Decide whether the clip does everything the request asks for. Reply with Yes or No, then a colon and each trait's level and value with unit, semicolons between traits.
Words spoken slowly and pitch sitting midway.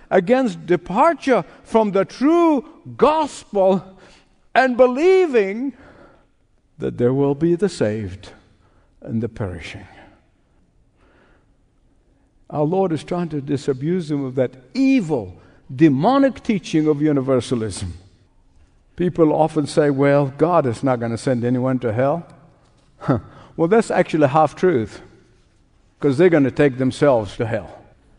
Yes: slow, 125 wpm; medium, 150 Hz